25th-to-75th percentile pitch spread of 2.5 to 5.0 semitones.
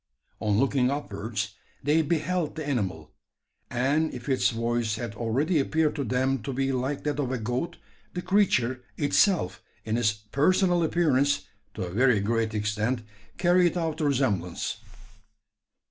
No: wide, 5.4 semitones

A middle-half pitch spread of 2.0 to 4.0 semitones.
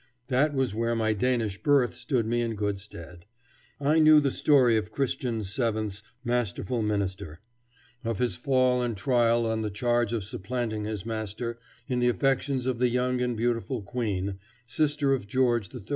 Yes: average, 3.1 semitones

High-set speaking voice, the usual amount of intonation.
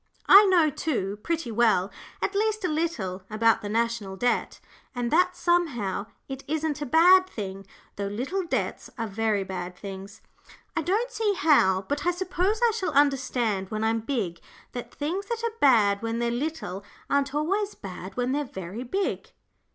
No: very high, 255 Hz; wide, 8.8 semitones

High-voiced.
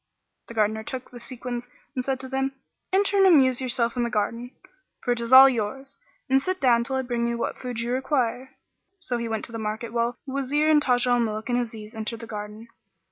Yes: high, 245 Hz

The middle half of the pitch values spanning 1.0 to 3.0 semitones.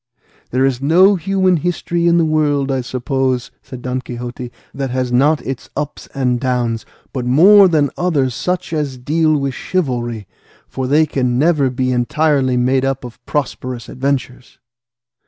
No: average, 3.7 semitones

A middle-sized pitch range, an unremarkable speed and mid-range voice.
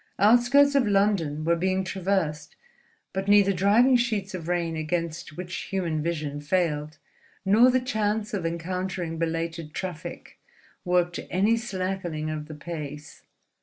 No: average, 3.7 semitones; slow, 130 wpm; medium, 180 Hz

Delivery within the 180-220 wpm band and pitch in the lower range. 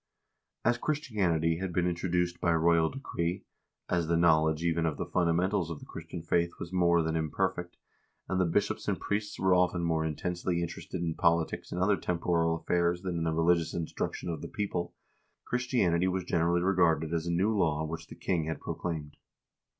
Yes: average, 190 wpm; very low, 85 Hz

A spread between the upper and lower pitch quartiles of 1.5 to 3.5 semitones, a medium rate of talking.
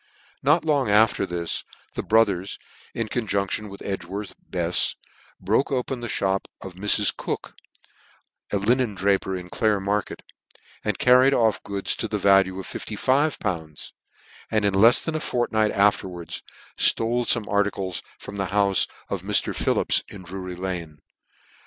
Yes: average, 2.9 semitones; average, 150 wpm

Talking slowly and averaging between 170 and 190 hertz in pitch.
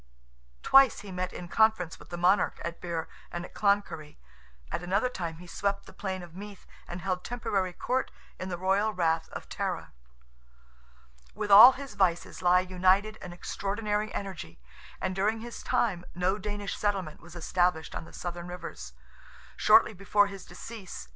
No: average, 165 wpm; medium, 185 Hz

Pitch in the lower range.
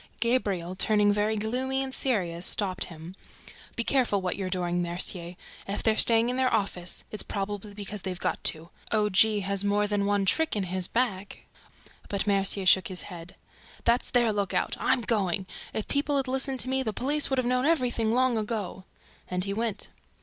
No: high, 205 Hz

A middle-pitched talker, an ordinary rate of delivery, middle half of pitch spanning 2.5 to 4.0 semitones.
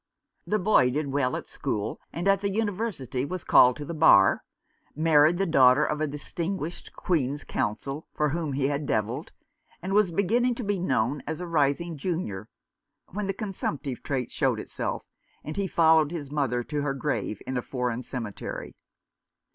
No: medium, 150 Hz; average, 170 wpm; average, 5.2 semitones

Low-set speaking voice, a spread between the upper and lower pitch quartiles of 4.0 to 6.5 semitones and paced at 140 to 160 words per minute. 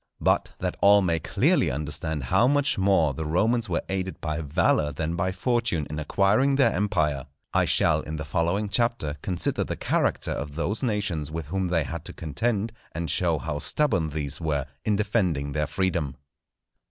No: very low, 85 Hz; average, 5.1 semitones; average, 175 wpm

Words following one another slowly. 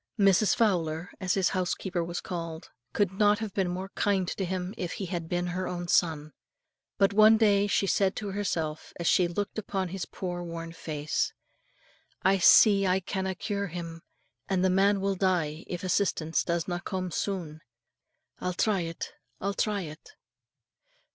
No: average, 165 wpm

